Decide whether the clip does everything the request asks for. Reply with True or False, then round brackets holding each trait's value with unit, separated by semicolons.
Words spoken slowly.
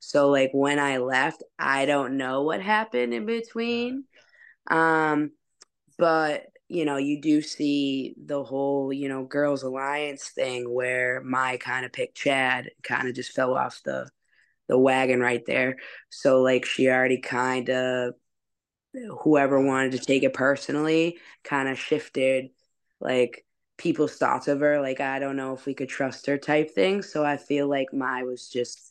False (165 wpm)